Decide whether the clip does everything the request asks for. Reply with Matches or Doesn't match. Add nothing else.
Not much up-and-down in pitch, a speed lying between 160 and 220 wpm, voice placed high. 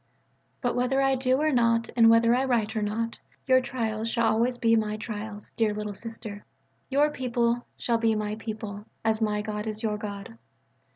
Matches